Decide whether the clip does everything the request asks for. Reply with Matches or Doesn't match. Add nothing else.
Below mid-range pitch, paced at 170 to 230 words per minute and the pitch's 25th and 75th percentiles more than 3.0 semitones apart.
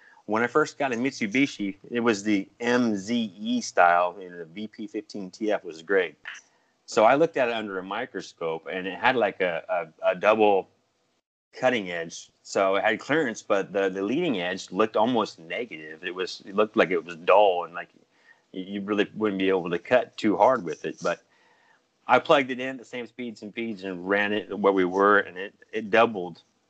Matches